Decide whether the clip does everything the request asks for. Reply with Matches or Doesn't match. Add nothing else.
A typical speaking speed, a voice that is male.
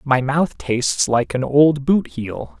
Matches